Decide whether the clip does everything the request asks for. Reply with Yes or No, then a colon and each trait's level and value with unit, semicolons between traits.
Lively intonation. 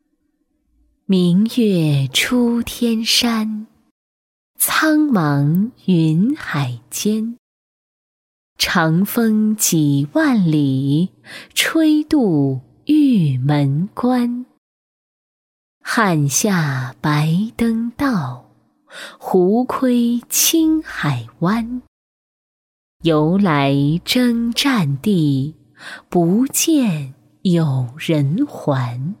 Yes: wide, 8.6 semitones